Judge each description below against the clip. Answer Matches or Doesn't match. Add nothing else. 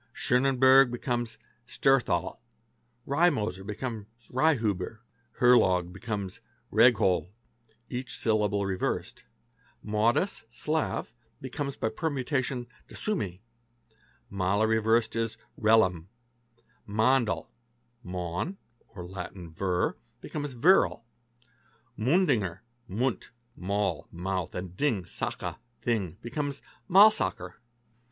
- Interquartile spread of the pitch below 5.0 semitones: Doesn't match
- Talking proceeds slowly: Matches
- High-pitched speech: Doesn't match